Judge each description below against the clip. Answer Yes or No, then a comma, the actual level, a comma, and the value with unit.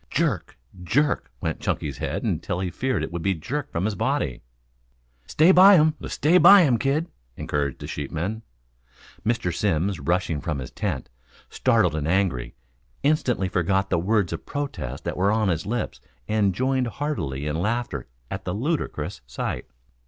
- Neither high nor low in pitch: No, low, 100 Hz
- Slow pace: No, average, 160 wpm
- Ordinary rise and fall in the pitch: No, wide, 8.0 semitones